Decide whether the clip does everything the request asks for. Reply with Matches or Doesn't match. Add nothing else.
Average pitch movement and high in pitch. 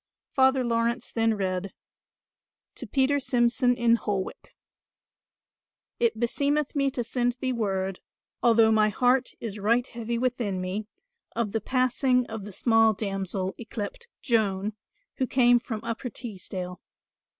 Matches